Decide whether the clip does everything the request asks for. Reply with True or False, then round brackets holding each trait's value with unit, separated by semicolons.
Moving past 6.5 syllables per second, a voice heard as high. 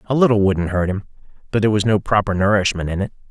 False (7.0 syllables/s; 100 Hz)